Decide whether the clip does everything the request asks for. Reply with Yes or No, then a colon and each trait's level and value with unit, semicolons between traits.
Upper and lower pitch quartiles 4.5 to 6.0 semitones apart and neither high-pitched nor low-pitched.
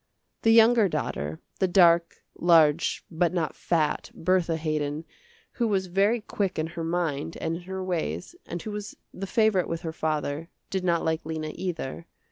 No: average, 3.0 semitones; medium, 170 Hz